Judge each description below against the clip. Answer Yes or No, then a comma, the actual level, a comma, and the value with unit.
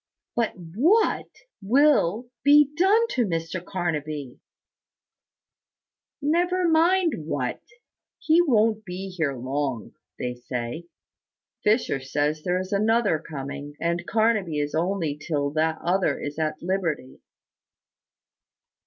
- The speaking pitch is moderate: Yes, medium, 175 Hz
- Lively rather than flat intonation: Yes, wide, 7.8 semitones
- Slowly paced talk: Yes, slow, 110 wpm